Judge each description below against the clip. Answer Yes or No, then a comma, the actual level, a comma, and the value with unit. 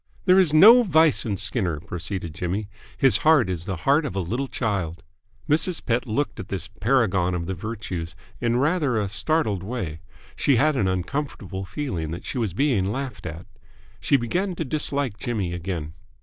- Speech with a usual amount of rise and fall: No, wide, 7.3 semitones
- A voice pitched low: Yes, low, 110 Hz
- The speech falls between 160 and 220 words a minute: Yes, average, 180 wpm